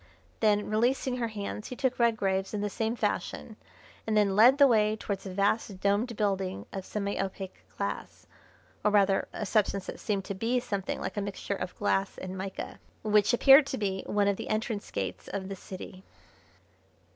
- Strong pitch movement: No, narrow, 2.4 semitones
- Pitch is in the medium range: No, high, 205 Hz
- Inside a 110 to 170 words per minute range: No, average, 185 wpm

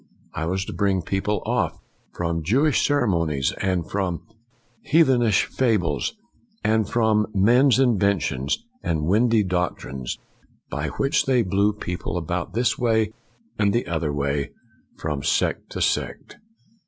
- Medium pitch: No, low, 100 Hz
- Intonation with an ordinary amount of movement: No, wide, 5.7 semitones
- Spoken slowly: Yes, slow, 130 wpm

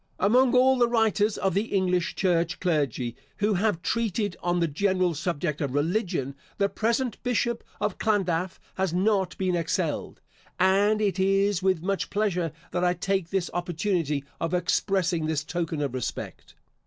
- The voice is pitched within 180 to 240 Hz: Yes, medium, 185 Hz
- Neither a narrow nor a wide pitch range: Yes, average, 3.5 semitones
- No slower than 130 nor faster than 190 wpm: Yes, average, 155 wpm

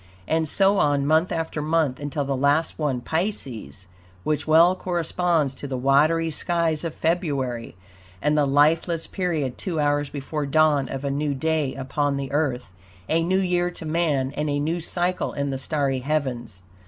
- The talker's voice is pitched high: No, medium, 150 Hz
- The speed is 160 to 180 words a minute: Yes, average, 170 wpm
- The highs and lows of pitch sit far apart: No, average, 3.0 semitones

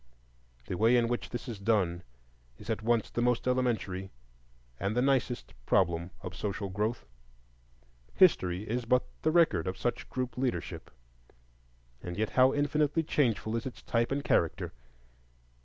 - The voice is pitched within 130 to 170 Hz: No, low, 115 Hz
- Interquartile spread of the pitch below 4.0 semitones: No, average, 4.7 semitones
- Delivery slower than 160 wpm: Yes, average, 150 wpm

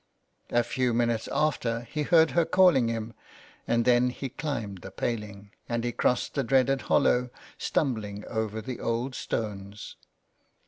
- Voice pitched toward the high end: No, low, 120 Hz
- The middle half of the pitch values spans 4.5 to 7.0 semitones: No, average, 3.1 semitones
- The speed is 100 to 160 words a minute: Yes, average, 145 wpm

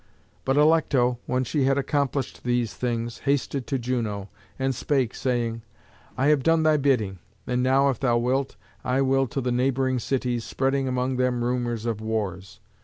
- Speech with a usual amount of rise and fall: No, narrow, 2.3 semitones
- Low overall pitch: Yes, low, 125 Hz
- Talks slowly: No, average, 170 wpm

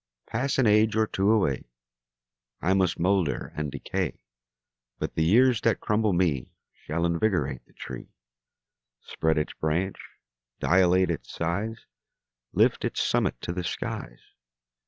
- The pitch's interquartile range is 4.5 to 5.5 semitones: Yes, average, 4.9 semitones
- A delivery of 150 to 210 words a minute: No, slow, 135 wpm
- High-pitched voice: No, very low, 90 Hz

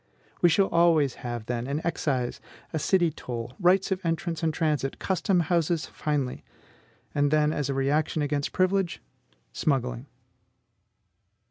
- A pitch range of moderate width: Yes, average, 3.9 semitones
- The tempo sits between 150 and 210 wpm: No, slow, 135 wpm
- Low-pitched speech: No, medium, 155 Hz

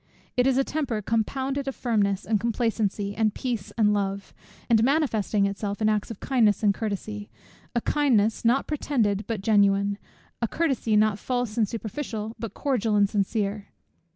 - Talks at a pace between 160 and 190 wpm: Yes, average, 165 wpm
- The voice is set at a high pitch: Yes, high, 220 Hz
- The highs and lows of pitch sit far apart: No, average, 3.2 semitones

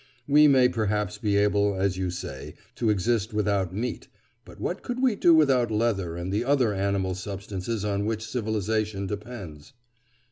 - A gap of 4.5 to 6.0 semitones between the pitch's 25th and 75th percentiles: No, average, 3.2 semitones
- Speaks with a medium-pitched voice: No, low, 105 Hz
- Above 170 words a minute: No, average, 165 wpm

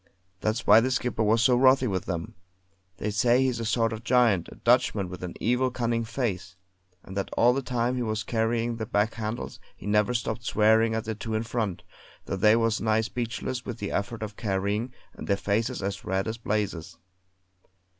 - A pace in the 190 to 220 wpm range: Yes, average, 200 wpm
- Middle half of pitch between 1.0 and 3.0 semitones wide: Yes, narrow, 2.4 semitones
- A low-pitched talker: Yes, low, 110 Hz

